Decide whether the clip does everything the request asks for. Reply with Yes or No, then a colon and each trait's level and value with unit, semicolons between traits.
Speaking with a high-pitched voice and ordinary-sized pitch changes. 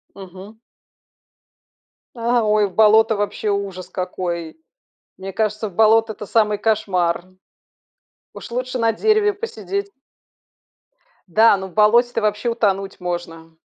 Yes: high, 210 Hz; average, 3.2 semitones